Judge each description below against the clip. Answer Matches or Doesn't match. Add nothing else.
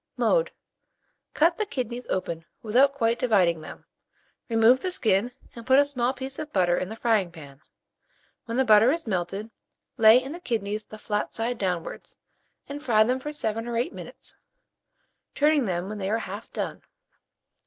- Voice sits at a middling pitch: Doesn't match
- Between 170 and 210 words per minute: Matches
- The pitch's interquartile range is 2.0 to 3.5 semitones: Doesn't match